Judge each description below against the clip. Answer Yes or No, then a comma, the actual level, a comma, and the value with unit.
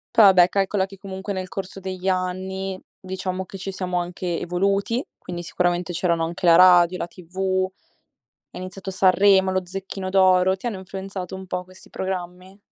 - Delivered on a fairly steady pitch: Yes, narrow, 1.0 semitones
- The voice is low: No, medium, 185 Hz